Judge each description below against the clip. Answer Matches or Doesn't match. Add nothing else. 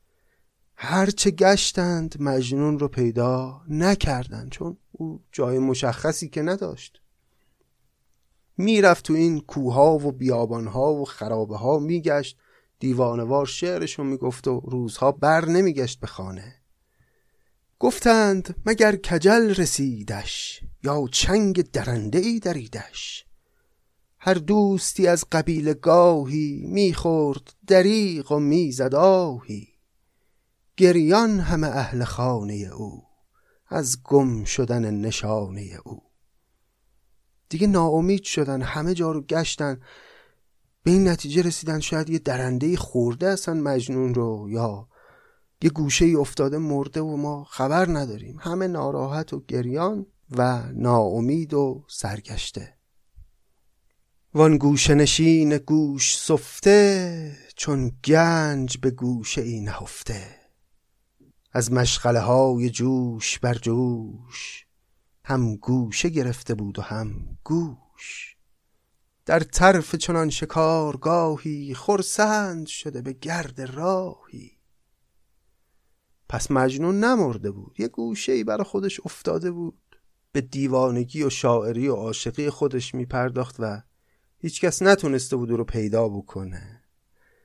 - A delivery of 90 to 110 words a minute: Matches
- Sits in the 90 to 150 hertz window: Matches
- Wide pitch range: Matches